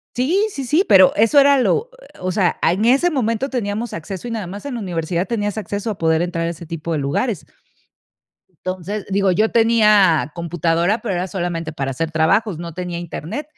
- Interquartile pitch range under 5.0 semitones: No, average, 5.3 semitones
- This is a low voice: No, high, 190 Hz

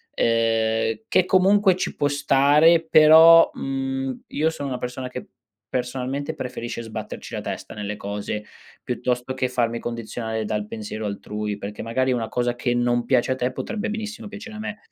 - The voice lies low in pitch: Yes, low, 125 Hz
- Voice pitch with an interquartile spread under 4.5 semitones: No, average, 5.0 semitones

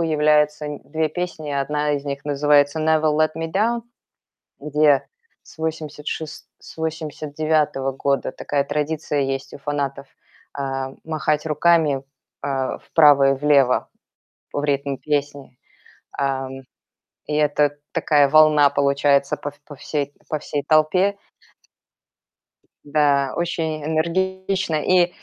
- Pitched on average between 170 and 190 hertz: No, medium, 150 Hz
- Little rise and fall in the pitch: Yes, narrow, 2.0 semitones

